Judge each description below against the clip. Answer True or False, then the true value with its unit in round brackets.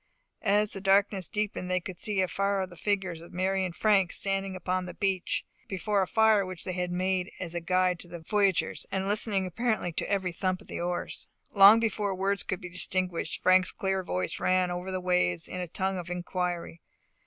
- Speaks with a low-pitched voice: False (185 Hz)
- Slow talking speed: False (205 wpm)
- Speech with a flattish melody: True (1.6 semitones)